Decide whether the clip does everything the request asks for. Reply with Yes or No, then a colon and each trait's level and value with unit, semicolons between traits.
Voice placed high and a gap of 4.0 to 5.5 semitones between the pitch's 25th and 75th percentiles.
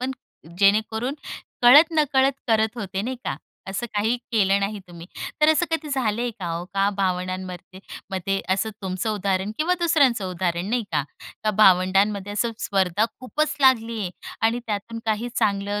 Yes: high, 210 Hz; average, 4.3 semitones